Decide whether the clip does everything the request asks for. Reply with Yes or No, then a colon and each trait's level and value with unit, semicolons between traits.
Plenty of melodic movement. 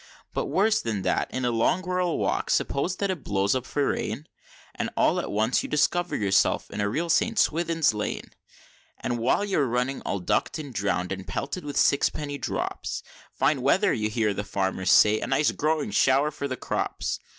Yes: wide, 7.1 semitones